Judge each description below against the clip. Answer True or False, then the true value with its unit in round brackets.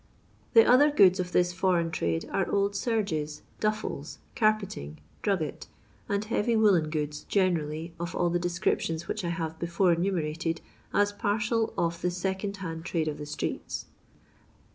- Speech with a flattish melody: False (3.9 semitones)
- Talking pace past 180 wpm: False (150 wpm)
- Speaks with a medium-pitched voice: True (175 Hz)